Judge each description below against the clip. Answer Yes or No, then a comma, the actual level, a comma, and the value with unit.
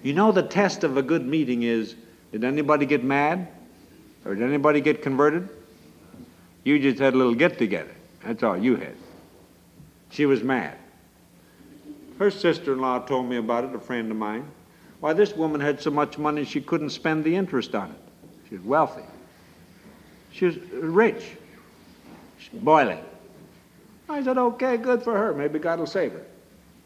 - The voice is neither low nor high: Yes, medium, 150 Hz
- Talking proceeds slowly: No, average, 170 wpm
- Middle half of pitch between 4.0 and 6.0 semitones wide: Yes, average, 5.2 semitones